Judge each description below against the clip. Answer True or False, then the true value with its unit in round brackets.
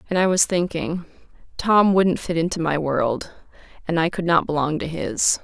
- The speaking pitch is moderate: True (170 Hz)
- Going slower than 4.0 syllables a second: False (5.0 syllables/s)